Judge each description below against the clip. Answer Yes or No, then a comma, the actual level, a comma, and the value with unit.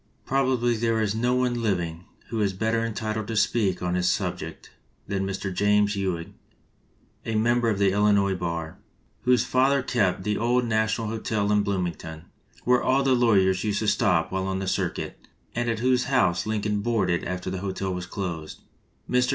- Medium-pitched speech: No, low, 105 Hz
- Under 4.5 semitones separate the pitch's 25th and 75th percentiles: Yes, average, 3.8 semitones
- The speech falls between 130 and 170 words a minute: No, average, 180 wpm